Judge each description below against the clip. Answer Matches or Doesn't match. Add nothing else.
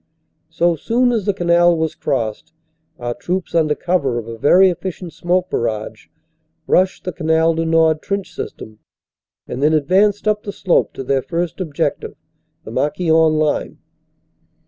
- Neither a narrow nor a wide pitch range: Matches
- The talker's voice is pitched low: Doesn't match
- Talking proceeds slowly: Doesn't match